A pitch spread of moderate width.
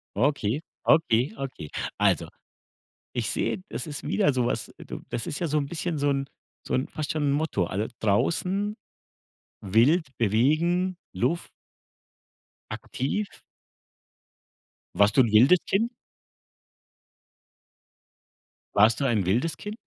No: wide, 6.6 semitones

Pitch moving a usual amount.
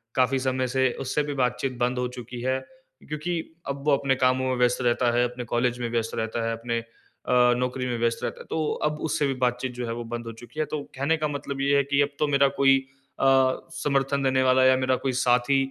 No: narrow, 2.2 semitones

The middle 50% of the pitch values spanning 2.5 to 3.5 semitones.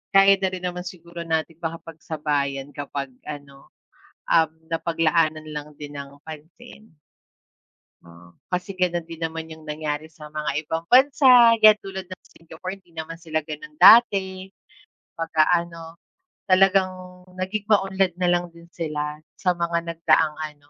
Yes: average, 3.2 semitones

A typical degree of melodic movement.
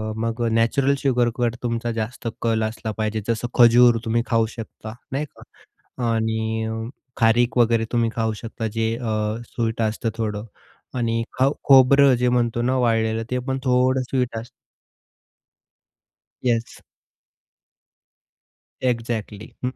No: narrow, 1.6 semitones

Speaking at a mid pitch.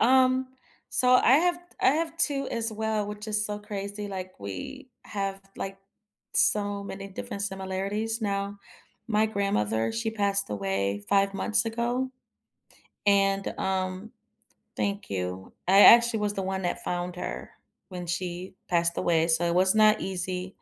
No: high, 200 Hz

